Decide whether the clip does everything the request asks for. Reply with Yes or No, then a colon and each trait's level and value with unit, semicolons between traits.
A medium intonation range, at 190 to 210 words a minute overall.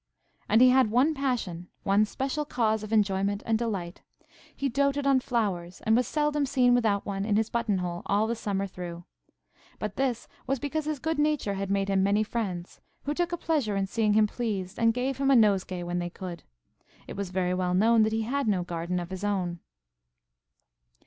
Yes: average, 5.0 semitones; average, 200 wpm